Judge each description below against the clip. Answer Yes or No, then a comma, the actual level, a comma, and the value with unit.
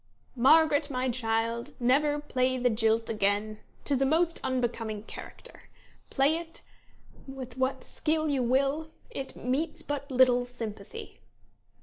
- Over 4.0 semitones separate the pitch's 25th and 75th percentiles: No, average, 3.7 semitones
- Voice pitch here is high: Yes, very high, 260 Hz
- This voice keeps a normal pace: No, slow, 125 wpm